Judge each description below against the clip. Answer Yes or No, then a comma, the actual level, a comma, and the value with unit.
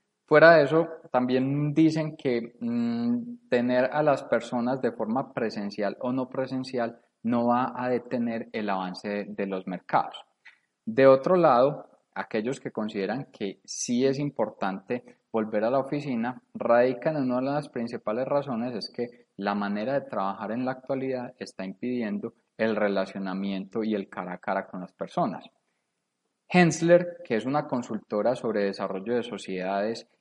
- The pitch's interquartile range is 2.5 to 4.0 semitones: No, average, 5.1 semitones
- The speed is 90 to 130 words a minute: No, average, 155 wpm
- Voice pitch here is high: No, low, 125 Hz